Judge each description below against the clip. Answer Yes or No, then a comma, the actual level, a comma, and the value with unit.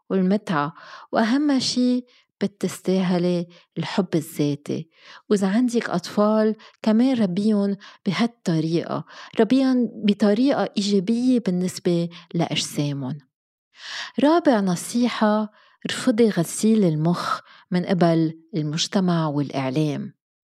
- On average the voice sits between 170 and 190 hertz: No, high, 200 Hz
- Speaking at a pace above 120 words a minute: No, average, 75 wpm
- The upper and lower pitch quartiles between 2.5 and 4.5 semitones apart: No, average, 5.1 semitones